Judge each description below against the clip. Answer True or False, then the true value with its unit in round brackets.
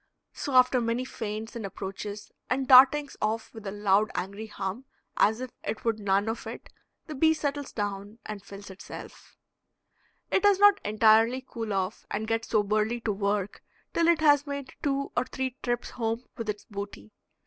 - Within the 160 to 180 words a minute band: True (175 wpm)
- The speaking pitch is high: True (225 Hz)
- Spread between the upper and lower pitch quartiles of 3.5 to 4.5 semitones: True (4.0 semitones)